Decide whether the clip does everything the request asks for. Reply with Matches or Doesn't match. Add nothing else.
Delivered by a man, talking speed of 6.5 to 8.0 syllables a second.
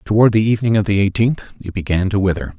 Matches